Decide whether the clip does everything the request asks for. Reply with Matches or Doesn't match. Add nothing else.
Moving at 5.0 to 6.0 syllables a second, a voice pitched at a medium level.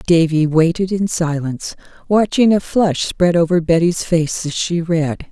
Doesn't match